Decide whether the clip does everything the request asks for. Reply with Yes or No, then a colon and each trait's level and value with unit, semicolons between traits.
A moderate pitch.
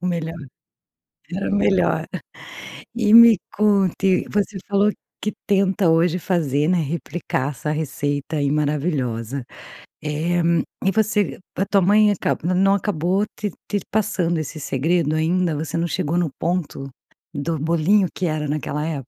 Yes: medium, 170 Hz